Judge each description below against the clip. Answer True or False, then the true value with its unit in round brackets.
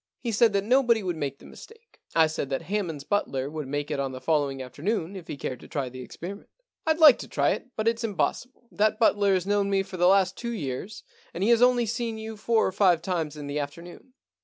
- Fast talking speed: True (255 wpm)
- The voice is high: True (195 Hz)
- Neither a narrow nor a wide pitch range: False (6.9 semitones)